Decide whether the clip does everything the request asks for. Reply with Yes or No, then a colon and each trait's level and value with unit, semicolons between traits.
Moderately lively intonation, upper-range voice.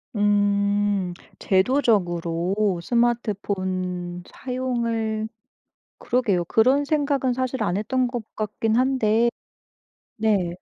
Yes: average, 4.6 semitones; high, 215 Hz